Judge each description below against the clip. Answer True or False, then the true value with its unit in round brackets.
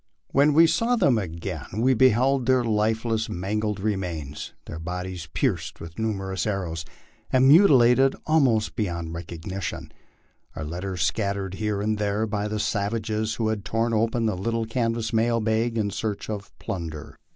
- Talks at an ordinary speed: True (155 wpm)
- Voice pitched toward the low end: True (110 Hz)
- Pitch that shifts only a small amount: False (3.3 semitones)